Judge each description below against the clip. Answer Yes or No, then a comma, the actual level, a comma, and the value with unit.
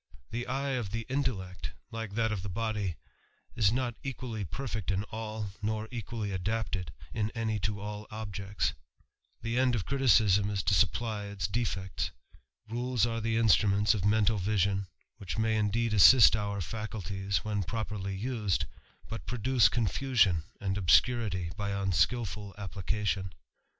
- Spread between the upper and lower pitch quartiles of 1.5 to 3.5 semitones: Yes, narrow, 2.6 semitones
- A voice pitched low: Yes, low, 105 Hz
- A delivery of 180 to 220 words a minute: No, average, 145 wpm